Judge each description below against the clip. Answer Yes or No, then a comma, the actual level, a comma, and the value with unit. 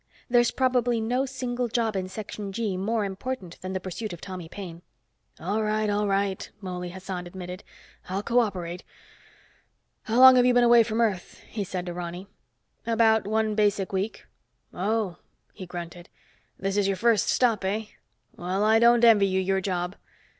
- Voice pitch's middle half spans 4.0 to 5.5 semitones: No, average, 3.5 semitones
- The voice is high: Yes, high, 200 Hz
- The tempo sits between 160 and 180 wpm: Yes, average, 170 wpm